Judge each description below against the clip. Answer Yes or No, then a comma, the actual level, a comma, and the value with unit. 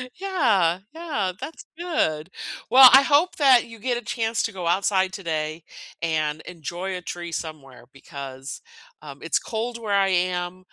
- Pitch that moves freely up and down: Yes, wide, 6.5 semitones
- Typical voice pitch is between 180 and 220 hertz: Yes, medium, 185 Hz